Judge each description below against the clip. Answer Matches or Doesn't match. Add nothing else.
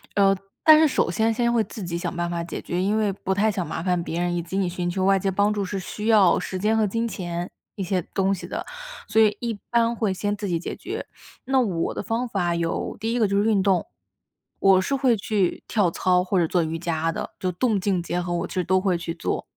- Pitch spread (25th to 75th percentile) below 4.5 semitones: Matches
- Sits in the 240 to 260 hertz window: Doesn't match